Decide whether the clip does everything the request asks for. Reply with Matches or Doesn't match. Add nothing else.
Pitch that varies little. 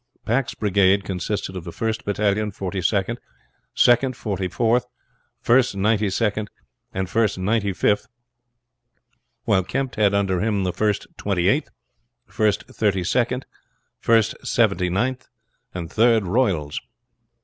Doesn't match